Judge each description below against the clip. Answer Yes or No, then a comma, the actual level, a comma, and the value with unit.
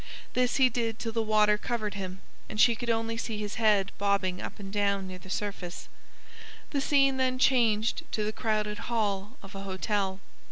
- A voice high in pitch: Yes, high, 210 Hz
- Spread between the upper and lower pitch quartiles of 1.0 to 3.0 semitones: Yes, narrow, 2.6 semitones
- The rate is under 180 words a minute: No, average, 190 wpm